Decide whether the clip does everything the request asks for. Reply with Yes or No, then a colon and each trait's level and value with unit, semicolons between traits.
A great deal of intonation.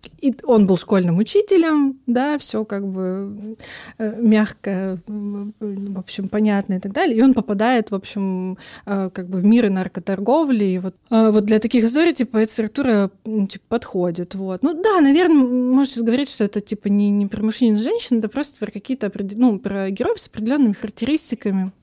No: average, 3.7 semitones